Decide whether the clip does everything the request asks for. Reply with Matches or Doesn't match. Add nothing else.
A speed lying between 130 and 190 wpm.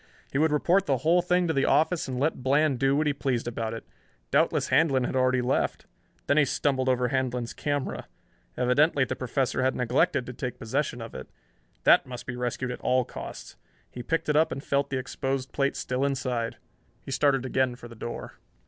Doesn't match